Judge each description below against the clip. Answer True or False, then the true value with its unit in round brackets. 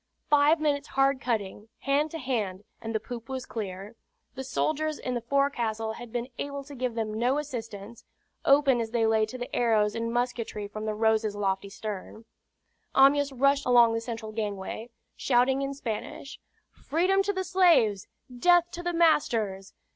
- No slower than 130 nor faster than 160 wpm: False (170 wpm)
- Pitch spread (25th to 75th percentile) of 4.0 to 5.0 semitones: True (4.3 semitones)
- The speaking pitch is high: True (240 Hz)